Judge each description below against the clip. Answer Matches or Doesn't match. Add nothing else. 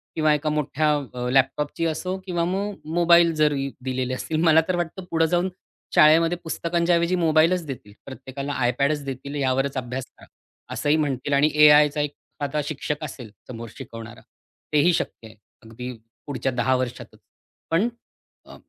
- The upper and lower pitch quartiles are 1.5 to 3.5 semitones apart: Doesn't match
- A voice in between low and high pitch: Matches